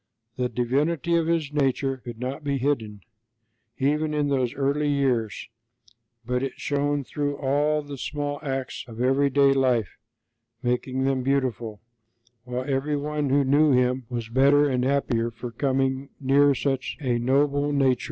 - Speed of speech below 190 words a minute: Yes, average, 150 wpm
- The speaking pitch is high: No, low, 135 Hz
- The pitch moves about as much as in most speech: No, narrow, 2.3 semitones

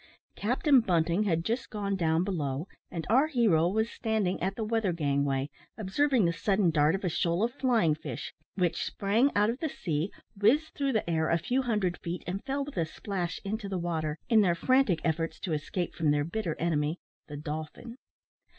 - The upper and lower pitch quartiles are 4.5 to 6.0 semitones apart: Yes, average, 5.3 semitones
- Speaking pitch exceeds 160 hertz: Yes, medium, 185 Hz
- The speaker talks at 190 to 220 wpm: Yes, average, 195 wpm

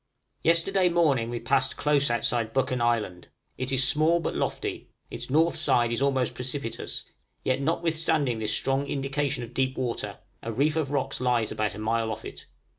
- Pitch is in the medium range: No, low, 130 Hz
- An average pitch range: Yes, average, 3.7 semitones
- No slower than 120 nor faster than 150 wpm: No, average, 180 wpm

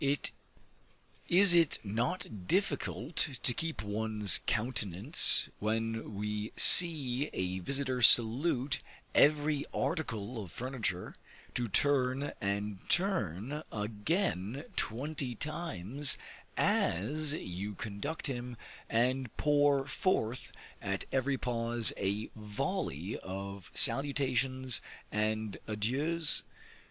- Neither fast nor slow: No, slow, 90 wpm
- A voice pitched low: Yes, low, 125 Hz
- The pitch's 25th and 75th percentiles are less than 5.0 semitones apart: No, wide, 5.5 semitones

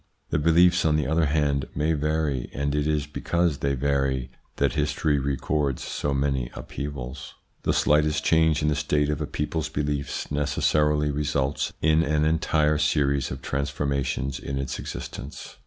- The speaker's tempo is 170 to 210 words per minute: No, average, 160 wpm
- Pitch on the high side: No, very low, 75 Hz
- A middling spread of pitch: No, narrow, 1.7 semitones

